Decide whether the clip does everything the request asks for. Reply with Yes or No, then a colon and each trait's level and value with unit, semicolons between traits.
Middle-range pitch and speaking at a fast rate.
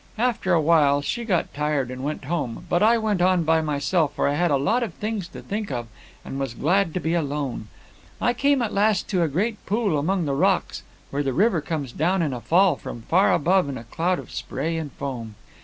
Yes: medium, 165 Hz; fast, 230 wpm